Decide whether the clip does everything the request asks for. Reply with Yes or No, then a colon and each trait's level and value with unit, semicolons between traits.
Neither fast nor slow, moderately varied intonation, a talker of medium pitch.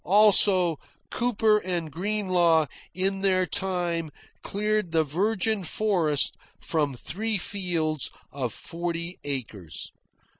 No: slow, 100 wpm; average, 4.1 semitones; medium, 180 Hz